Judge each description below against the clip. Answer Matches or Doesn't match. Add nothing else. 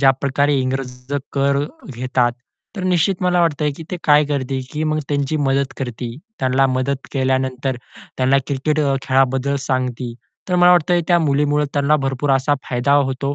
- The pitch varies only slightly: Matches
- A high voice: Doesn't match